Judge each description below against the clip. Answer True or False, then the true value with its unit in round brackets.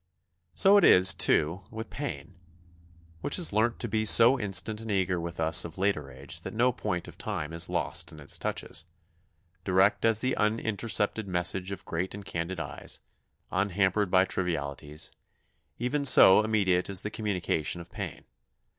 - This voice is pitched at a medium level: False (95 Hz)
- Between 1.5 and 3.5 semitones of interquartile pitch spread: False (4.0 semitones)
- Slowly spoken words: False (165 wpm)